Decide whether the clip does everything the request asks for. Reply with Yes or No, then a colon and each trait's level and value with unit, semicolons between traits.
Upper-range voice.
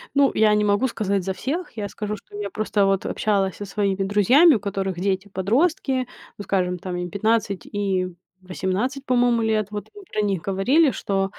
Yes: high, 205 Hz